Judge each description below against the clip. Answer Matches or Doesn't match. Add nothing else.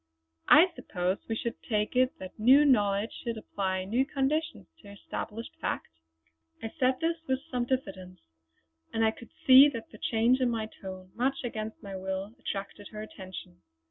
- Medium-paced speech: Matches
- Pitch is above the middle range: Matches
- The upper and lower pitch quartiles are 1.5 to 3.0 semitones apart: Doesn't match